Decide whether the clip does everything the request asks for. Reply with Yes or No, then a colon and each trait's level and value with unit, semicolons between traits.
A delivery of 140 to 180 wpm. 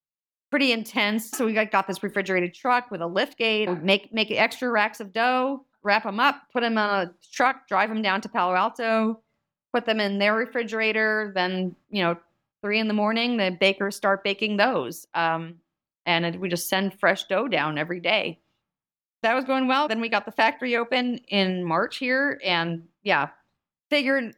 No: average, 190 wpm